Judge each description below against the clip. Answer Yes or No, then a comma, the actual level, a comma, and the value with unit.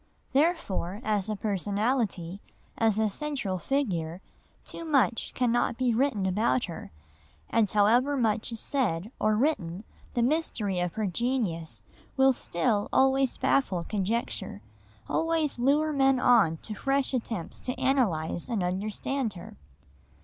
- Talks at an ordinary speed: No, slow, 130 wpm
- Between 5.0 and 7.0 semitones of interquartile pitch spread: Yes, wide, 5.5 semitones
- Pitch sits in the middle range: No, high, 225 Hz